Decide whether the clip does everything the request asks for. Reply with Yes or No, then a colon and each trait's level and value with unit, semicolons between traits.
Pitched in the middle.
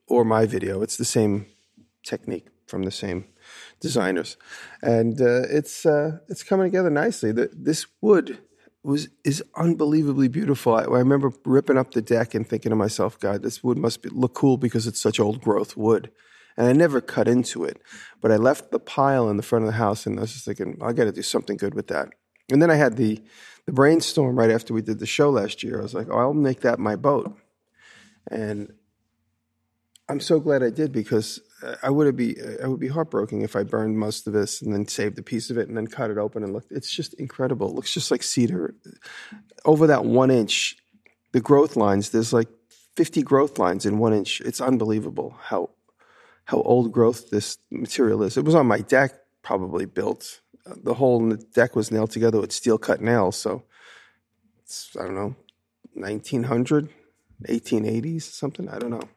No: low, 115 Hz